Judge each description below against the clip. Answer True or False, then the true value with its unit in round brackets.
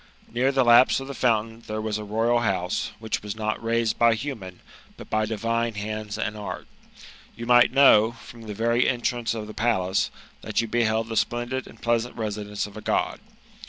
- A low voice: True (115 Hz)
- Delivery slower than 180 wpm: False (195 wpm)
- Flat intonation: True (1.8 semitones)